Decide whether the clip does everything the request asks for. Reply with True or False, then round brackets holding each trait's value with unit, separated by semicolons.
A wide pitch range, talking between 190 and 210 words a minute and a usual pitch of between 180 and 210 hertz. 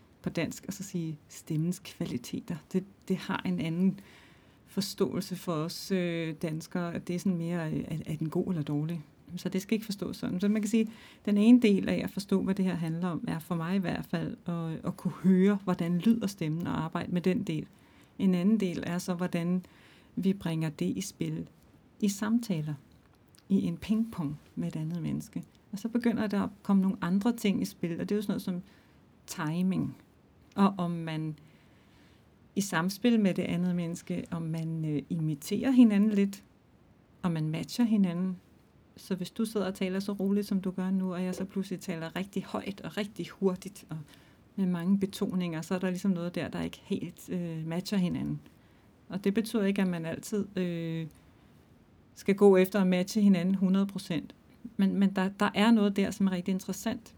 False (2.8 semitones; 195 wpm; 185 Hz)